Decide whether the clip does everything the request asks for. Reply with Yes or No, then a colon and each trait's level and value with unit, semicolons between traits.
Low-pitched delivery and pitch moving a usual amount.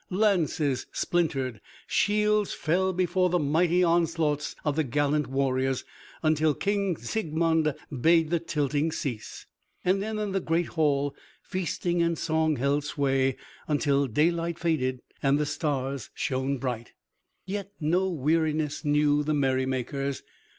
No: medium, 155 Hz; average, 3.6 semitones